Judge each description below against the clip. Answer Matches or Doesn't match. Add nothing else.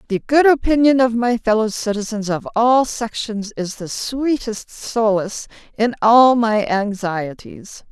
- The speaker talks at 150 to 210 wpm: Doesn't match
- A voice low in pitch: Doesn't match